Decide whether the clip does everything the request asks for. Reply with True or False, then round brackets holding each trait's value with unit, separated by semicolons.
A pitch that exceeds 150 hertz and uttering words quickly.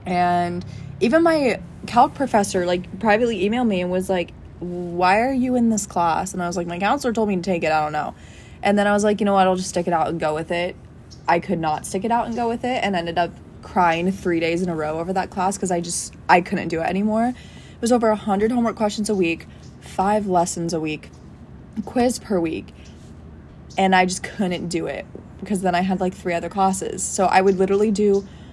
True (185 Hz; 240 wpm)